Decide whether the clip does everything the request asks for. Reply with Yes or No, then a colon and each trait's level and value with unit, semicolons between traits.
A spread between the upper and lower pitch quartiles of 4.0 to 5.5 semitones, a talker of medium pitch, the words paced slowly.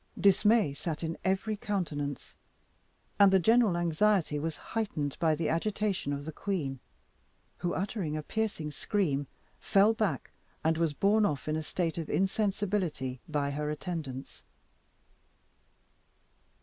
Yes: average, 5.2 semitones; medium, 170 Hz; slow, 130 wpm